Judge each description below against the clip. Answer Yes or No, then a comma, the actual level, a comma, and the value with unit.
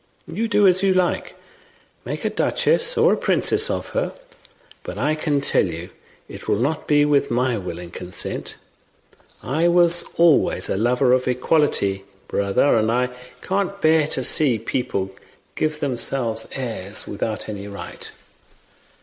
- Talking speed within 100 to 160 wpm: Yes, average, 150 wpm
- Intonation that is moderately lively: No, wide, 7.6 semitones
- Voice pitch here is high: No, low, 135 Hz